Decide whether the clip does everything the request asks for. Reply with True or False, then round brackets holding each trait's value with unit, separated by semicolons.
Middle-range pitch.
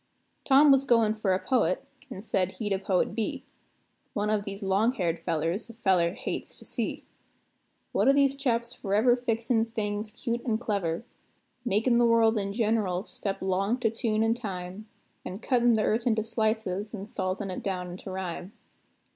False (215 Hz)